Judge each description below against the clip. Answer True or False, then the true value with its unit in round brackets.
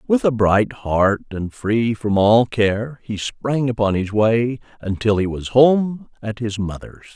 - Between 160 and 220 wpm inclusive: True (175 wpm)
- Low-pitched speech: True (115 Hz)